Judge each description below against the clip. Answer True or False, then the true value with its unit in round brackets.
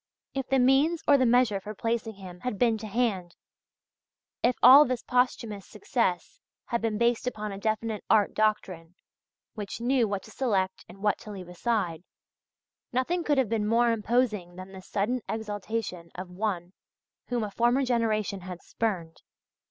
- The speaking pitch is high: True (220 Hz)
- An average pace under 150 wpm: False (165 wpm)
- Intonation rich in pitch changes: False (4.0 semitones)